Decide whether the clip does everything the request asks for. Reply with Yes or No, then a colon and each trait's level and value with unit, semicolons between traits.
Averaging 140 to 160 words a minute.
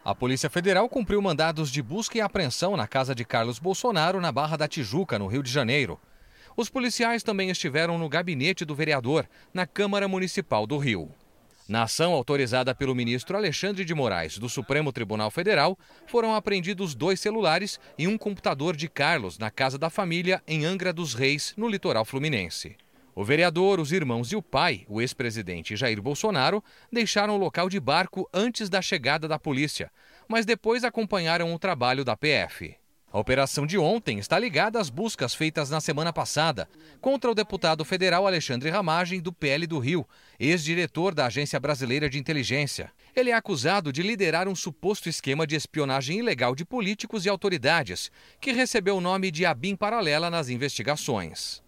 No: average, 170 wpm